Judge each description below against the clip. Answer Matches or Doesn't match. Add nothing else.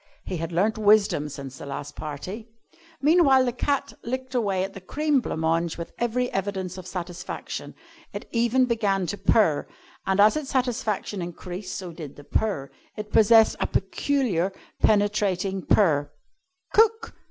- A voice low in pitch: Doesn't match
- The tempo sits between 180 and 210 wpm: Doesn't match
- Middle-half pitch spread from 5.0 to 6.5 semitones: Matches